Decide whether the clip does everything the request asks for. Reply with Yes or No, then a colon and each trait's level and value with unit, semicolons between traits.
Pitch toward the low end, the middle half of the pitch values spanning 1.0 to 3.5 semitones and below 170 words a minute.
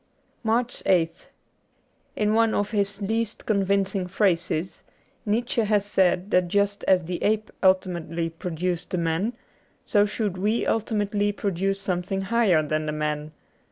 No: high, 195 Hz; average, 3.0 semitones; average, 150 wpm